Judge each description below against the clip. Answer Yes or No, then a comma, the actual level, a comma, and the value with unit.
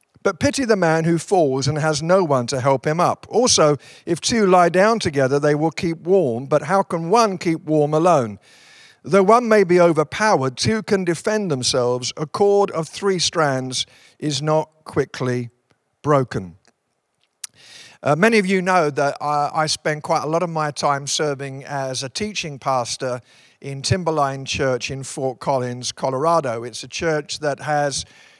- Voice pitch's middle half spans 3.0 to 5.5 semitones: Yes, average, 4.4 semitones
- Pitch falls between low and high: Yes, medium, 150 Hz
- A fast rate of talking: No, average, 170 wpm